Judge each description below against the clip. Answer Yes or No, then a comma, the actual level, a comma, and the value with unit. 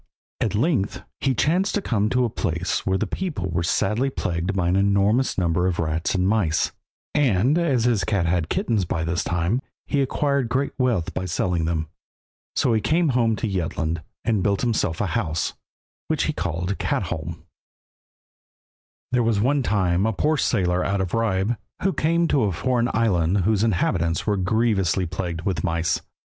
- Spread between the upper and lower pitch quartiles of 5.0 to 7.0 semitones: Yes, wide, 5.5 semitones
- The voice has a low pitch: Yes, low, 100 Hz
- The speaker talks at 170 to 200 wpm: Yes, average, 175 wpm